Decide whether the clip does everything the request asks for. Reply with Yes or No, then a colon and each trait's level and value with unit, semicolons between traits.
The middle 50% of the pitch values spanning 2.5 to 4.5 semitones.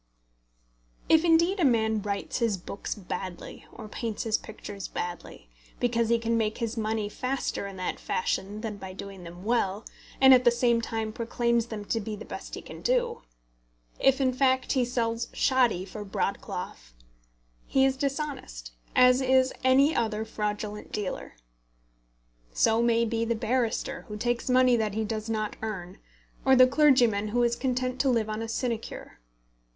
Yes: average, 3.3 semitones